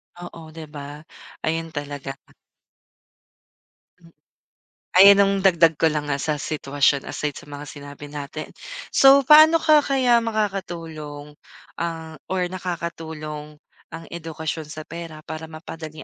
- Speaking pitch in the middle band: Yes, medium, 160 Hz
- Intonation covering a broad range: No, average, 3.4 semitones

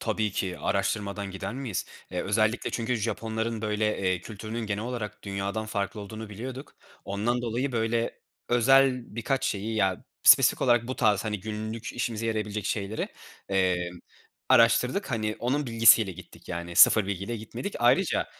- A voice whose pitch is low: Yes, low, 110 Hz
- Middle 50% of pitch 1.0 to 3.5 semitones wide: Yes, average, 2.8 semitones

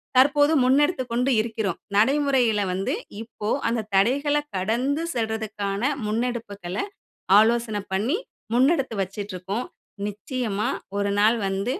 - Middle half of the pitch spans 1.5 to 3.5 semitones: No, average, 4.1 semitones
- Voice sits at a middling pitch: No, high, 225 Hz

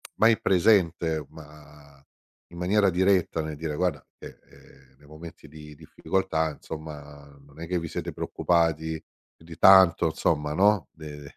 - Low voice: Yes, very low, 80 Hz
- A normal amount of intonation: Yes, average, 3.1 semitones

